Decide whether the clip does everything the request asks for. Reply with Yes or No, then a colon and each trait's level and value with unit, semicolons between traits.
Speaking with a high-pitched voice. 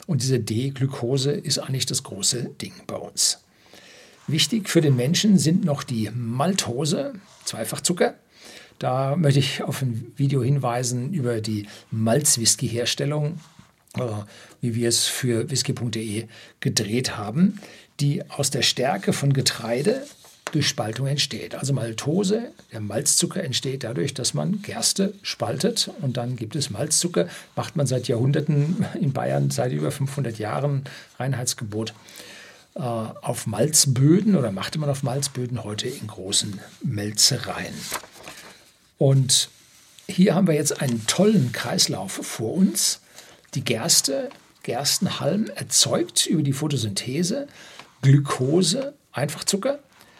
No: low, 135 Hz